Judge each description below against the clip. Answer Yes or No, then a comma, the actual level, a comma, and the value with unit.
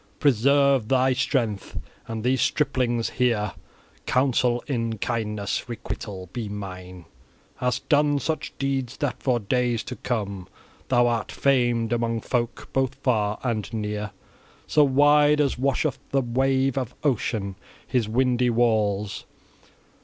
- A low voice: Yes, low, 120 Hz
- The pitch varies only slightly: No, average, 3.6 semitones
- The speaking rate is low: Yes, slow, 125 wpm